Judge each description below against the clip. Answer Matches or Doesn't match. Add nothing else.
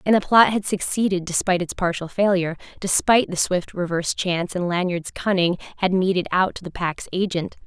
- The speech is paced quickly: Doesn't match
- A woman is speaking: Matches